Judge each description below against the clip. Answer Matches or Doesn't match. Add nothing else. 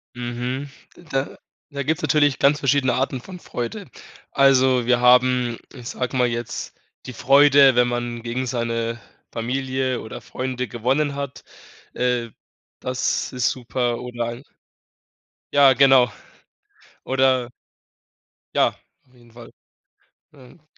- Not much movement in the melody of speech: Matches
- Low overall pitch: Matches